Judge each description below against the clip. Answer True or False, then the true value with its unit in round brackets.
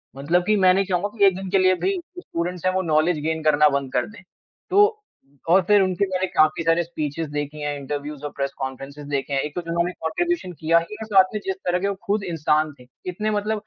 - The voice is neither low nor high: True (170 Hz)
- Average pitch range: True (4.1 semitones)